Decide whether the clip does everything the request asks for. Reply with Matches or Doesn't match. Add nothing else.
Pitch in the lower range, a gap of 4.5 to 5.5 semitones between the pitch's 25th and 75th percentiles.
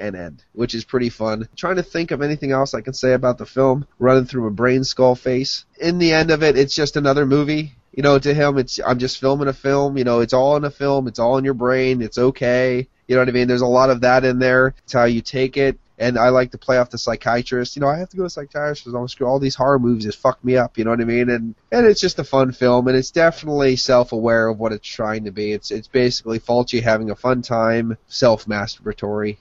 Doesn't match